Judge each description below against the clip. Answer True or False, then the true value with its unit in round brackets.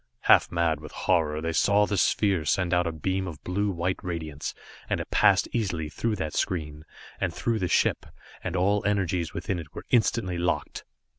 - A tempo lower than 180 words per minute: False (190 wpm)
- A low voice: True (90 Hz)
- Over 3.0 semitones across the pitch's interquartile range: True (3.5 semitones)